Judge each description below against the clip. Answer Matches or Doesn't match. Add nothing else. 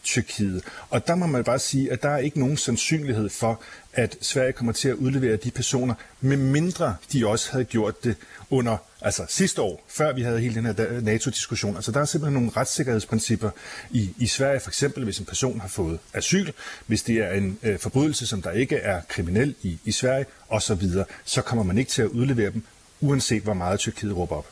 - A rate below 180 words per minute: Doesn't match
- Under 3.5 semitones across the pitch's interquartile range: Doesn't match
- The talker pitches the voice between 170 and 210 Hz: Doesn't match